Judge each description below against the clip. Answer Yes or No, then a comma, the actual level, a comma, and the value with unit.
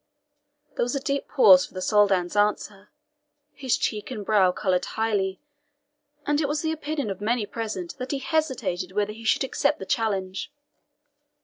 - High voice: Yes, high, 220 Hz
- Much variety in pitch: Yes, wide, 6.0 semitones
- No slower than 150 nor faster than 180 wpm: Yes, average, 170 wpm